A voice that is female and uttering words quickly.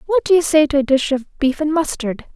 Yes: female; fast, 280 wpm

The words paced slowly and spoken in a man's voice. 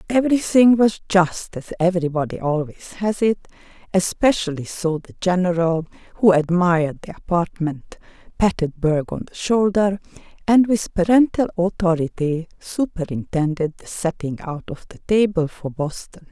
No: slow, 125 wpm; female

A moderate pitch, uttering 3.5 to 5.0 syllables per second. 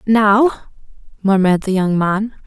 No: high, 205 Hz; 4.0 syllables/s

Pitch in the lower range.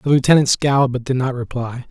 Yes: low, 130 Hz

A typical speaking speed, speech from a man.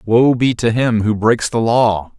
No: fast, 220 wpm; male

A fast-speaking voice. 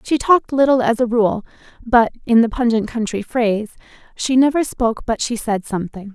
No: average, 185 wpm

